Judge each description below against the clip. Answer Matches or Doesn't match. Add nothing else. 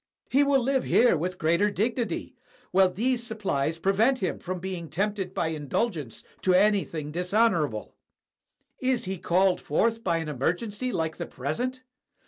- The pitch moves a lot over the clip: Matches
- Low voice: Doesn't match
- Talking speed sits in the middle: Matches